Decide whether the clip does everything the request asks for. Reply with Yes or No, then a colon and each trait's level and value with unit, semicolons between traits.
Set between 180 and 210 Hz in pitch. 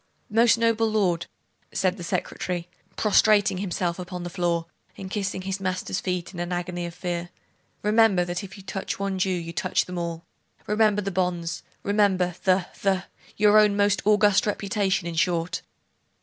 Yes: medium, 185 Hz